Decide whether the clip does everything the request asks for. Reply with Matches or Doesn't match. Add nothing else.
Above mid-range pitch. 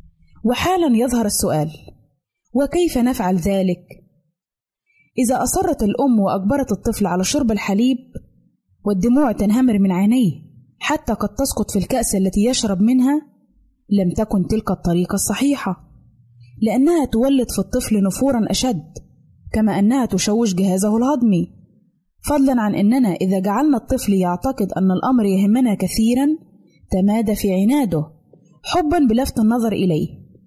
Matches